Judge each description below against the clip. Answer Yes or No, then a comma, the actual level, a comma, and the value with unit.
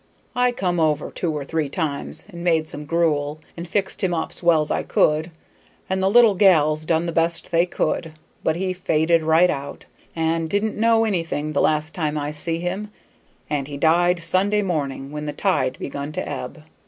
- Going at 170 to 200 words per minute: Yes, average, 190 wpm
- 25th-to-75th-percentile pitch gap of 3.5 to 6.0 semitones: No, average, 3.0 semitones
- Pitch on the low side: No, medium, 165 Hz